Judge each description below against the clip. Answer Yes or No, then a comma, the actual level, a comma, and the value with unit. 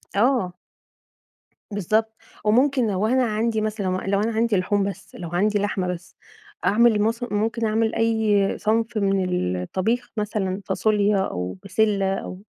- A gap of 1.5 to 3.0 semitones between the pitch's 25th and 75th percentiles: Yes, narrow, 2.4 semitones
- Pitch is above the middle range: Yes, high, 210 Hz